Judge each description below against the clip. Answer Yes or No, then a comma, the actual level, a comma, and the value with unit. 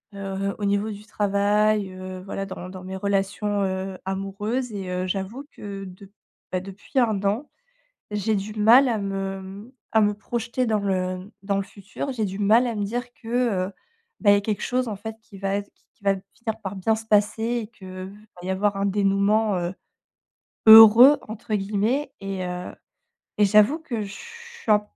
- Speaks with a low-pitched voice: No, high, 205 Hz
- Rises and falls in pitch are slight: Yes, narrow, 2.3 semitones